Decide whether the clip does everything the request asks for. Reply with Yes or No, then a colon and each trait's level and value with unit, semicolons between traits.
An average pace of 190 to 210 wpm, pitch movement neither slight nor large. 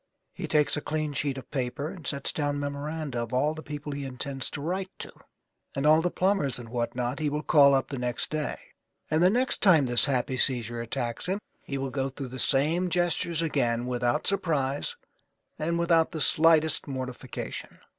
Yes: average, 195 wpm; average, 3.5 semitones